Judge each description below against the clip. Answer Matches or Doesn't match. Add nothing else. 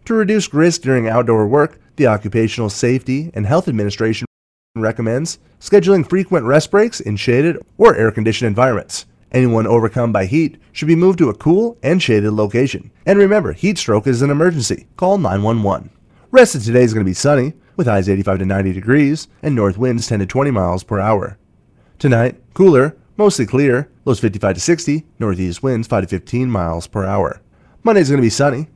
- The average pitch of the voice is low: Matches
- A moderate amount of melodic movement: Doesn't match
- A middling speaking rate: Matches